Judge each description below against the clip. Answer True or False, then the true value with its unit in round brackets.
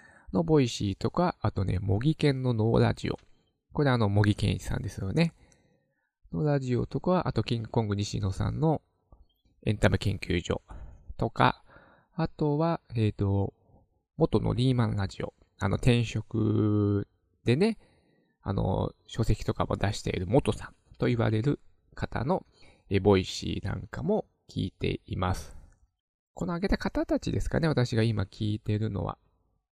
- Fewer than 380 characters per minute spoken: True (290 characters per minute)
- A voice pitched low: True (110 Hz)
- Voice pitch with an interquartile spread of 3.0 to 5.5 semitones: True (5.2 semitones)